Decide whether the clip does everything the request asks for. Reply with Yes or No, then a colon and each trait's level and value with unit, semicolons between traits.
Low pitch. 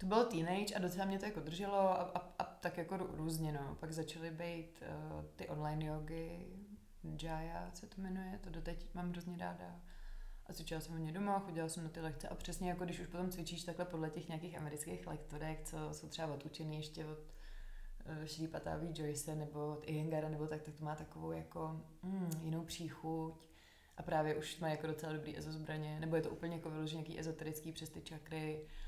No: medium, 160 Hz